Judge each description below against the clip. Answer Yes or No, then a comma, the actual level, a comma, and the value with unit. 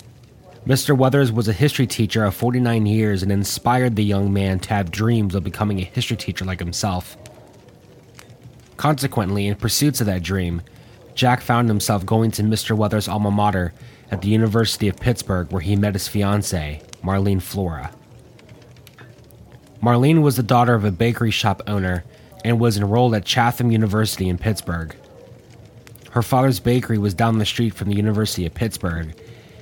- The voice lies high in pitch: No, low, 110 Hz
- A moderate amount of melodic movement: Yes, average, 3.4 semitones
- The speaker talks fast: No, average, 160 wpm